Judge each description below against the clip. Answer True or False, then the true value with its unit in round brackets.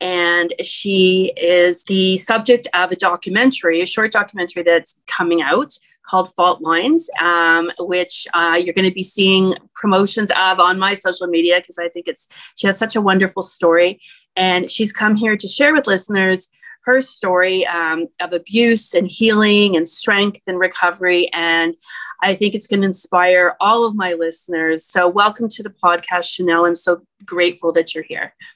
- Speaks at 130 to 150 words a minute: False (175 wpm)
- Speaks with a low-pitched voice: False (185 Hz)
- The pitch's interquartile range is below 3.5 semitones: True (3.0 semitones)